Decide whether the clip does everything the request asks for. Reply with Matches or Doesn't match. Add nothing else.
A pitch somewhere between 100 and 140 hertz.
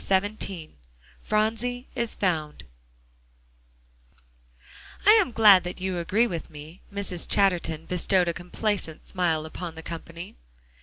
Doesn't match